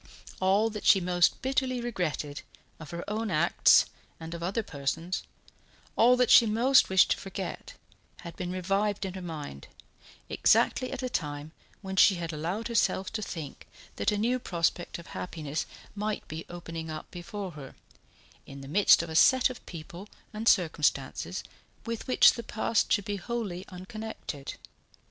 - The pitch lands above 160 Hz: Yes, medium, 185 Hz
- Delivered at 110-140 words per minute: No, average, 165 wpm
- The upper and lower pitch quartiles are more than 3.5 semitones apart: Yes, average, 4.8 semitones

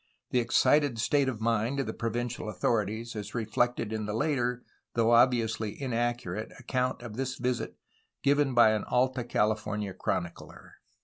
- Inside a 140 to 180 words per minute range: Yes, average, 150 wpm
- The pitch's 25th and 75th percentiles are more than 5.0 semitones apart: No, narrow, 2.5 semitones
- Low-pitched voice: Yes, low, 120 Hz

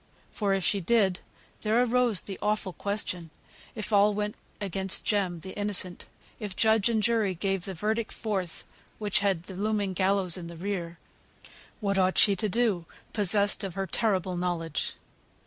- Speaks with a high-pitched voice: Yes, high, 200 Hz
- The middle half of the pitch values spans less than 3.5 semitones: Yes, narrow, 2.4 semitones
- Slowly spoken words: No, average, 165 wpm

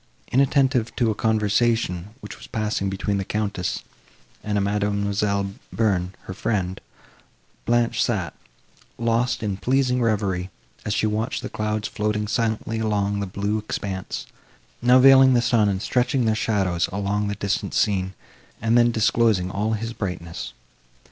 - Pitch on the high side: No, low, 105 Hz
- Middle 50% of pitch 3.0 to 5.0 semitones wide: No, narrow, 2.6 semitones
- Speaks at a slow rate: No, average, 145 wpm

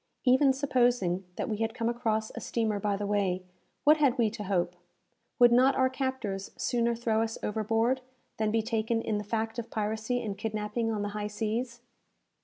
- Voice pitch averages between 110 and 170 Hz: No, high, 225 Hz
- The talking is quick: No, average, 190 wpm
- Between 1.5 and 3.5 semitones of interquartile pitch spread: Yes, narrow, 2.5 semitones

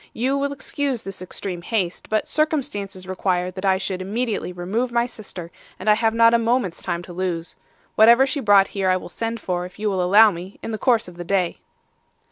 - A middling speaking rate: No, fast, 215 wpm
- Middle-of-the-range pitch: No, high, 200 Hz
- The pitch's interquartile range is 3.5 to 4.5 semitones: Yes, average, 4.1 semitones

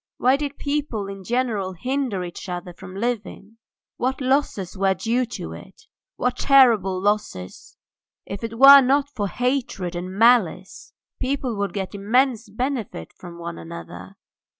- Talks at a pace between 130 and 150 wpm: Yes, average, 145 wpm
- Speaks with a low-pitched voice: No, high, 215 Hz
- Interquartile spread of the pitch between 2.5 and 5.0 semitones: No, wide, 5.5 semitones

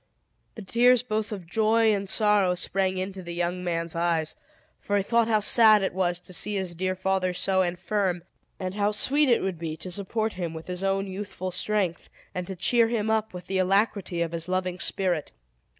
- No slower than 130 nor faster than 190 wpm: No, average, 200 wpm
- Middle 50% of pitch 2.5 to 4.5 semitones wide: Yes, average, 2.8 semitones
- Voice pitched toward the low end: No, high, 190 Hz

